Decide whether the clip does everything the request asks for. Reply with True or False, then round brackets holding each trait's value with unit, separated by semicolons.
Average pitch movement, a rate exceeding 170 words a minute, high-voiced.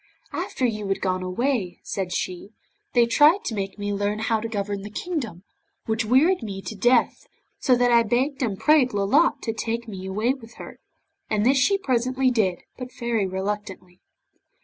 True (4.1 semitones; 180 wpm; 225 Hz)